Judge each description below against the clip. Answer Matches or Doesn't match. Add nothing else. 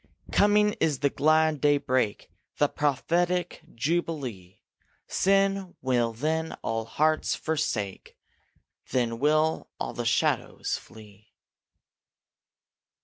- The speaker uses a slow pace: Matches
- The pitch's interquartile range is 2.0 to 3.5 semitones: Doesn't match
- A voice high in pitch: Doesn't match